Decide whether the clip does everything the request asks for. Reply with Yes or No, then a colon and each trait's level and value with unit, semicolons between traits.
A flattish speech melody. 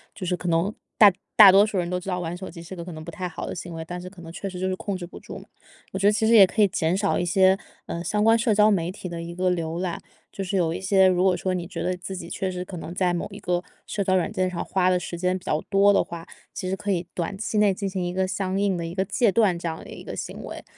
Yes: narrow, 2.0 semitones